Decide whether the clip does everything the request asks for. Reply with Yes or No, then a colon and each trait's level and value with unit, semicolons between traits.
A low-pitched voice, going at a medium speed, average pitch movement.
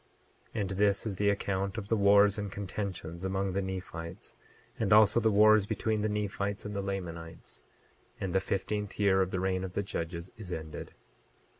No: low, 100 Hz; average, 185 wpm; narrow, 1.7 semitones